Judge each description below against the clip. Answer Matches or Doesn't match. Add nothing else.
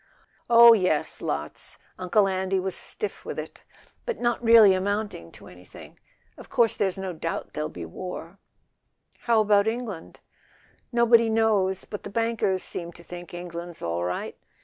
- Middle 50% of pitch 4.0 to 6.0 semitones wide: Matches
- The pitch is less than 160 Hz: Doesn't match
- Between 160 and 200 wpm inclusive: Doesn't match